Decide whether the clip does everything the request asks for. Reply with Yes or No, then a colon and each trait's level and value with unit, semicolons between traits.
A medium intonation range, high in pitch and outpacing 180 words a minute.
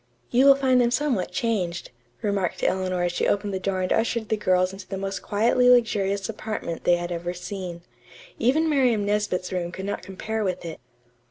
Yes: average, 3.7 semitones; high, 195 Hz; average, 190 wpm